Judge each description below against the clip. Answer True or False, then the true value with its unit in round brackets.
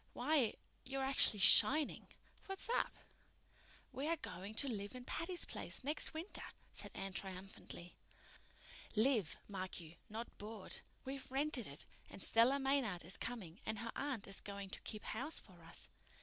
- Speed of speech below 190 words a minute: True (155 wpm)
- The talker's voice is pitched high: True (230 Hz)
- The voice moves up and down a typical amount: False (5.9 semitones)